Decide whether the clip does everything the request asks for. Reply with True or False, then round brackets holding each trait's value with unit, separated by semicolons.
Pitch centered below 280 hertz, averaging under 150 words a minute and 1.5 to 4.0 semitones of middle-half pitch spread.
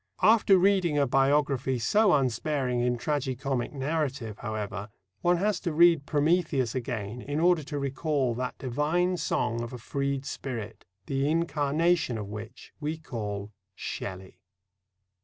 False (140 Hz; 140 wpm; 4.7 semitones)